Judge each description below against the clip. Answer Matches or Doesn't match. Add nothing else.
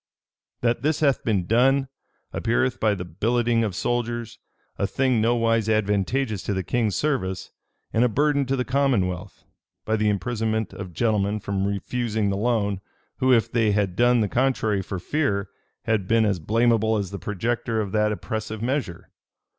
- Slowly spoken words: Doesn't match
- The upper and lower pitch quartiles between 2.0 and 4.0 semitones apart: Matches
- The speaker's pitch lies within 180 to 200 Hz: Doesn't match